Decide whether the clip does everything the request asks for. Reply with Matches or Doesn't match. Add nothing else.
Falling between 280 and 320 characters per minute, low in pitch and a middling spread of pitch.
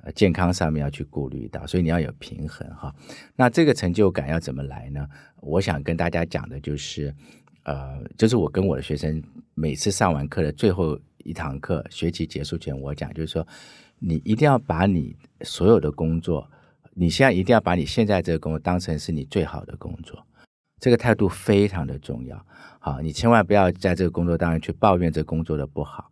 Matches